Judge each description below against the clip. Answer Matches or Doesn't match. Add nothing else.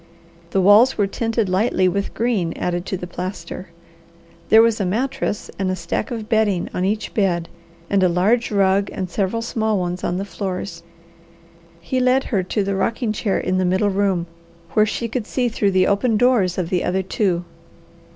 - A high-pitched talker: Matches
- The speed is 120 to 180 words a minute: Doesn't match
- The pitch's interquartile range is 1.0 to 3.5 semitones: Matches